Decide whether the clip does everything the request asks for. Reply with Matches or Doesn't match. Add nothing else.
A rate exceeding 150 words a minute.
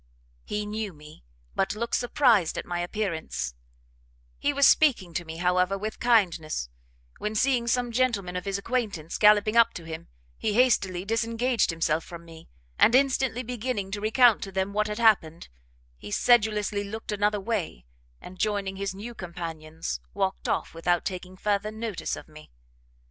Matches